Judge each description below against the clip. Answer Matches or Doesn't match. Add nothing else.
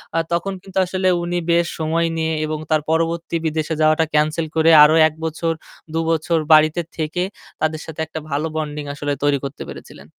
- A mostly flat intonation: Matches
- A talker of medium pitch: Matches